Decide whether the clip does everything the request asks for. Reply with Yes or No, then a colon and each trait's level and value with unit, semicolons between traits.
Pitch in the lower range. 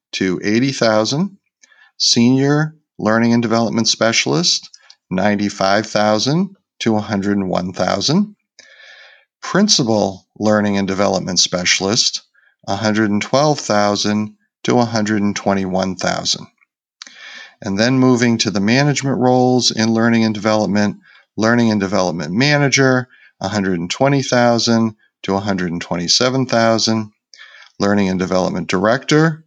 Yes: low, 110 Hz